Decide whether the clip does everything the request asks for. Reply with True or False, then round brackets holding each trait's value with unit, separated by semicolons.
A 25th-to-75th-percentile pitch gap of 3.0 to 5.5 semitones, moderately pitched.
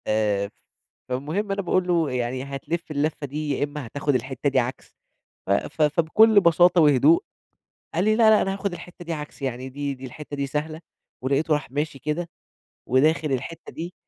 True (4.2 semitones; 150 Hz)